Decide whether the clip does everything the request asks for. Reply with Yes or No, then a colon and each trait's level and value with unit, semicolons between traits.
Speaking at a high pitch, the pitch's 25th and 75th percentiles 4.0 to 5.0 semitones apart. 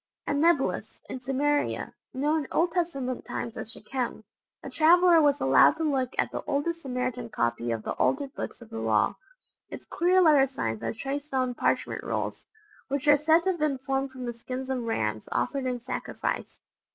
No: very high, 270 Hz; average, 3.4 semitones